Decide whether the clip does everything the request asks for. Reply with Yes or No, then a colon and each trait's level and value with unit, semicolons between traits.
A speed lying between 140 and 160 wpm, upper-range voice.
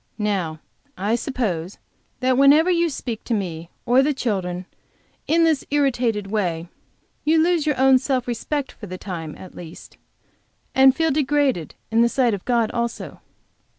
Yes: average, 155 wpm; high, 240 Hz